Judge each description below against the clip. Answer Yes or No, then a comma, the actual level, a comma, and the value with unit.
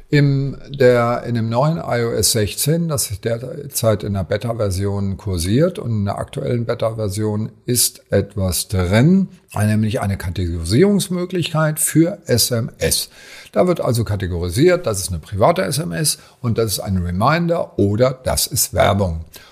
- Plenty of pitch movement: Yes, wide, 6.4 semitones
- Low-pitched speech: Yes, low, 115 Hz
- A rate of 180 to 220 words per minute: No, average, 140 wpm